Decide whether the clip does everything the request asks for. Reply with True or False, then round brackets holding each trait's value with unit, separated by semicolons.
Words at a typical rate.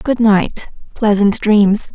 False (125 wpm)